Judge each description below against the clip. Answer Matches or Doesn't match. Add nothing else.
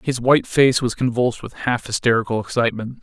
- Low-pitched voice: Matches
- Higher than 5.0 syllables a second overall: Matches